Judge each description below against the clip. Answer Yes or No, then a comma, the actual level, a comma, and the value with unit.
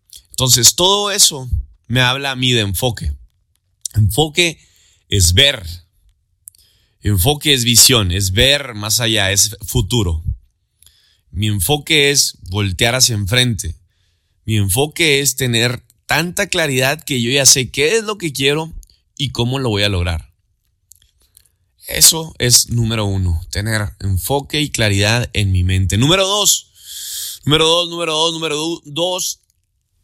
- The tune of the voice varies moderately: No, wide, 7.0 semitones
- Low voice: Yes, low, 110 Hz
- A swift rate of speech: No, average, 140 wpm